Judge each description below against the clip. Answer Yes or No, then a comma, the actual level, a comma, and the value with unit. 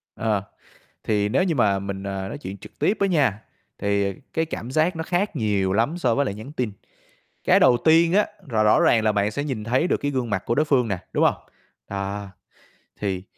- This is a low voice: Yes, low, 115 Hz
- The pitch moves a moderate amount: No, wide, 6.7 semitones